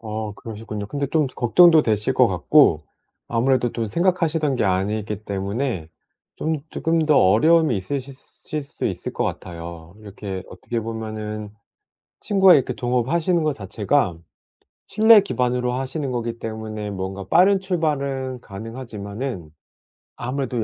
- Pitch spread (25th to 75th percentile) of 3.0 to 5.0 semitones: No, wide, 5.4 semitones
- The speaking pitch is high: No, low, 120 Hz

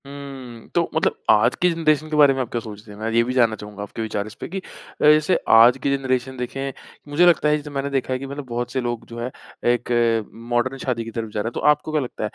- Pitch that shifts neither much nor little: Yes, average, 3.5 semitones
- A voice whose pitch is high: No, low, 125 Hz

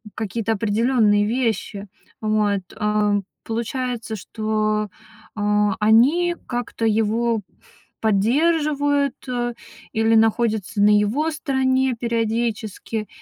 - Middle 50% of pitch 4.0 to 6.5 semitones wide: No, average, 2.8 semitones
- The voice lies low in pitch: No, high, 225 Hz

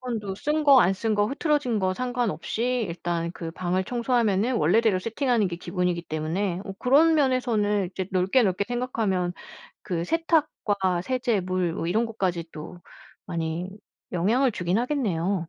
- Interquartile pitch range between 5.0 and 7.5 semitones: Yes, wide, 5.6 semitones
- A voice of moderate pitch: No, high, 200 Hz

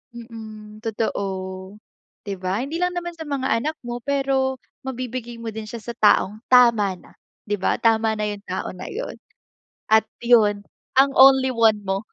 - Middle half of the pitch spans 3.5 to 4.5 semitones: Yes, average, 4.0 semitones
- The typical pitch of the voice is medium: No, high, 230 Hz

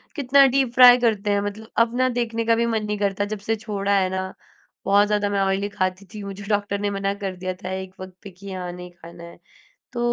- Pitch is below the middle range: No, high, 205 Hz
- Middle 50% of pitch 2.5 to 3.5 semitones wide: Yes, average, 2.9 semitones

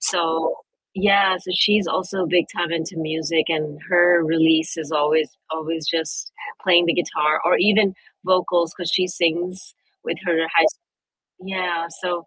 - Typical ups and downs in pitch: No, narrow, 2.2 semitones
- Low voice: No, medium, 170 Hz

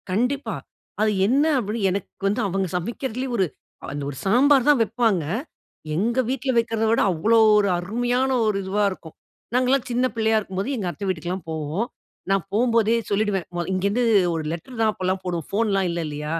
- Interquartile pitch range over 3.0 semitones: Yes, average, 4.3 semitones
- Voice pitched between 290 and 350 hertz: No, high, 210 Hz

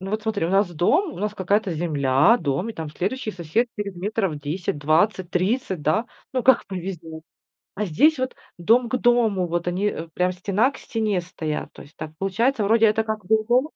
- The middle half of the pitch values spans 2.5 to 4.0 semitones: No, average, 4.6 semitones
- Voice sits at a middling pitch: No, high, 195 Hz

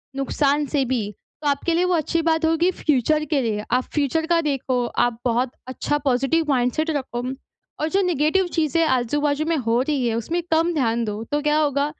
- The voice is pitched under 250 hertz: No, very high, 290 Hz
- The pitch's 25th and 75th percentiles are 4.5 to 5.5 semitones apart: No, average, 4.1 semitones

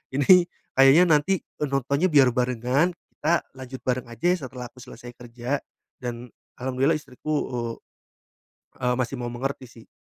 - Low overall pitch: Yes, low, 130 Hz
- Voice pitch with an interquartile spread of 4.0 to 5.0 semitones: No, average, 3.0 semitones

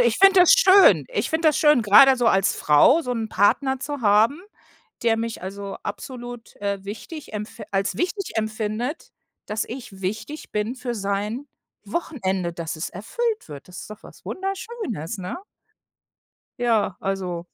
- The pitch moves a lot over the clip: Yes, wide, 6.4 semitones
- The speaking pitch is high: Yes, high, 225 Hz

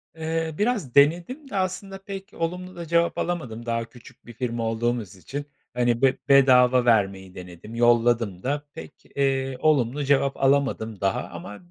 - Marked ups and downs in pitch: Yes, wide, 5.8 semitones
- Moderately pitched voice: No, low, 130 Hz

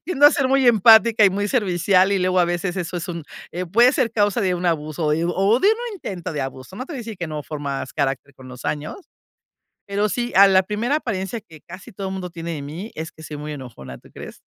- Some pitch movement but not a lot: No, wide, 5.7 semitones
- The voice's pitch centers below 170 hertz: No, medium, 185 Hz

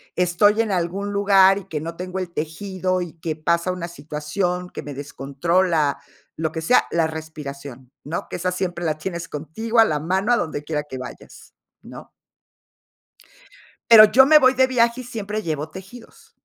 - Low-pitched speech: No, medium, 175 Hz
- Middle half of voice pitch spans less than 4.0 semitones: No, average, 4.4 semitones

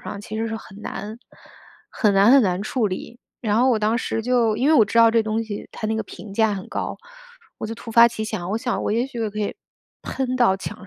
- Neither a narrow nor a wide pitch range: No, narrow, 1.9 semitones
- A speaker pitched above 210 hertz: Yes, high, 220 Hz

